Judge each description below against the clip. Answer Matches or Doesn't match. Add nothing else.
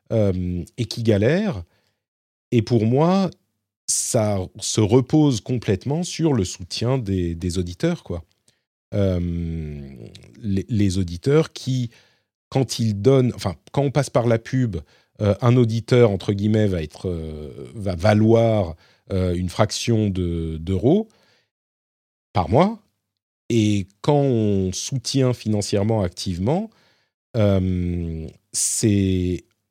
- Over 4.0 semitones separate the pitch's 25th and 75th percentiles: Matches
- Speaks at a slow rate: Matches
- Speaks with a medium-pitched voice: Doesn't match